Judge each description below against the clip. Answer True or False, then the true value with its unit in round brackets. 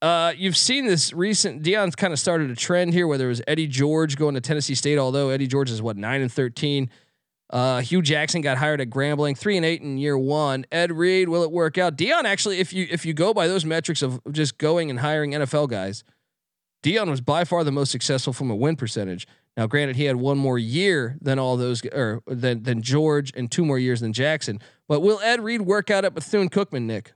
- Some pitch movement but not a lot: True (4.6 semitones)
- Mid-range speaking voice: True (150 Hz)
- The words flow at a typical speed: False (235 wpm)